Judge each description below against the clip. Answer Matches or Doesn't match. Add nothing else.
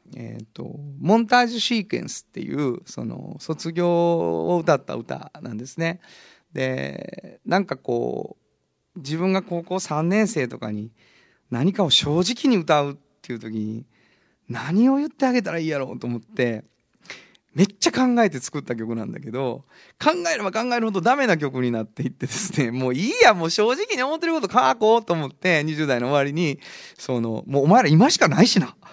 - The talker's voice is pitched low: Doesn't match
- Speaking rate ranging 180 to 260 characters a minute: Doesn't match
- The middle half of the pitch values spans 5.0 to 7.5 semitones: Doesn't match